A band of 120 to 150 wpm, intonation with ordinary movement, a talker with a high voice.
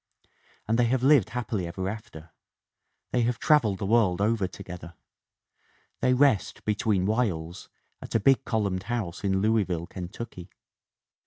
No: average, 145 wpm; average, 4.3 semitones; low, 105 Hz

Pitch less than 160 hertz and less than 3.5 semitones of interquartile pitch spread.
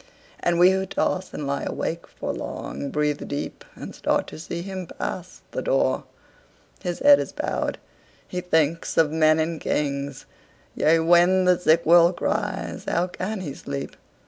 No: medium, 170 Hz; average, 2.9 semitones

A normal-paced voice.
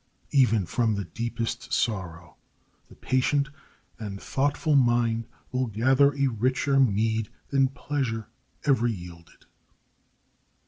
No: slow, 105 wpm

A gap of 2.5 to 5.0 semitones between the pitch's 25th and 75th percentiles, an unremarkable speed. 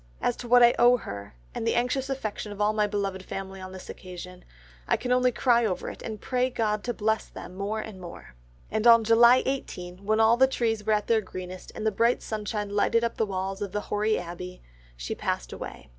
No: average, 3.6 semitones; fast, 225 wpm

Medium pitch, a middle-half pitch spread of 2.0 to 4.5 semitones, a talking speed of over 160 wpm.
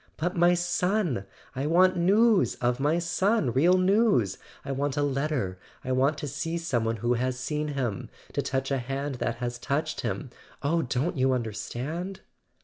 No: medium, 145 Hz; wide, 5.4 semitones; average, 175 wpm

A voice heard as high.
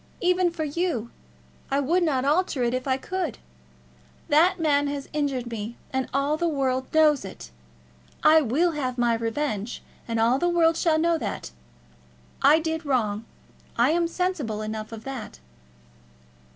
Yes: very high, 285 Hz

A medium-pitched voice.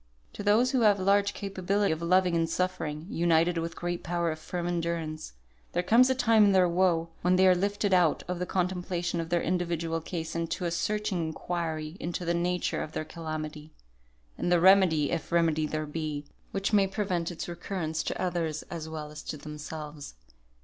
Yes: medium, 170 Hz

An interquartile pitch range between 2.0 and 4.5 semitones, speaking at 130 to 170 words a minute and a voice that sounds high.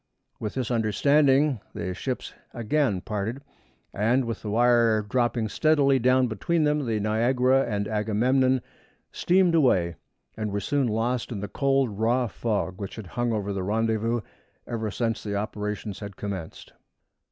No: average, 3.6 semitones; average, 150 wpm; low, 115 Hz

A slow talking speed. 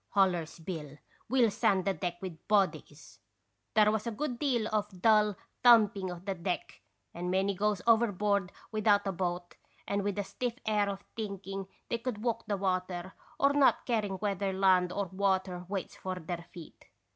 No: average, 185 wpm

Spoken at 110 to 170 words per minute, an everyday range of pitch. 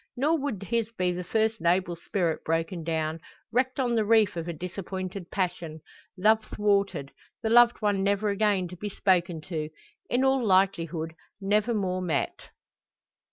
Yes: average, 160 wpm; average, 4.1 semitones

